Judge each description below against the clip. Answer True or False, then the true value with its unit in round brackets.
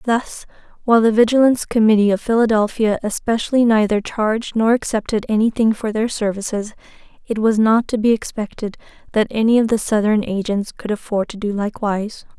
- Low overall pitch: False (220 Hz)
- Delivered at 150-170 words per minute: True (160 wpm)